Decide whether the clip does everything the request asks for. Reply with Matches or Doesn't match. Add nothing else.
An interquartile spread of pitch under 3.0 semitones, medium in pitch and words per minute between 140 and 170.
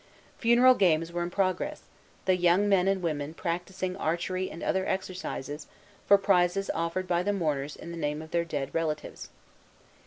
Matches